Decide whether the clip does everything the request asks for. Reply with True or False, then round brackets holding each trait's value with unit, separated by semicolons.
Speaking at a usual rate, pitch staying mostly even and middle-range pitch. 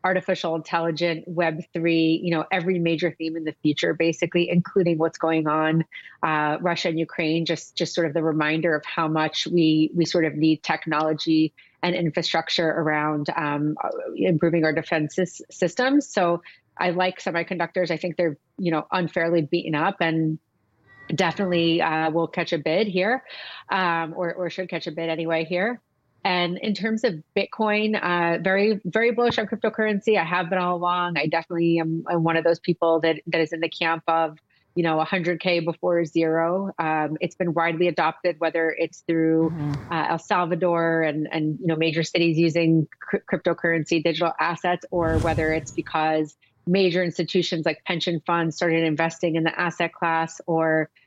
True (175 wpm; 1.6 semitones; 170 Hz)